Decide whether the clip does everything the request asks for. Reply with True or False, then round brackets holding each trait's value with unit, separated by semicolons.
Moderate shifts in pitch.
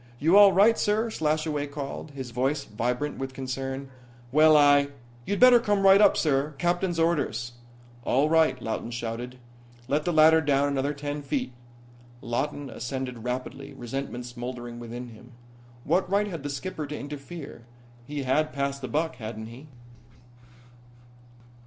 True (3.9 semitones)